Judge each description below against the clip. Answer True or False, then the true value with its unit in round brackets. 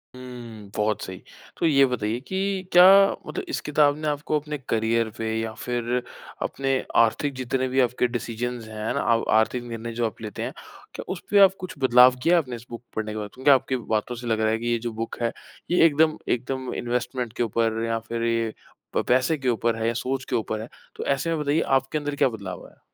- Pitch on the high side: False (120 Hz)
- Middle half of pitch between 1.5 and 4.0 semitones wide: True (3.3 semitones)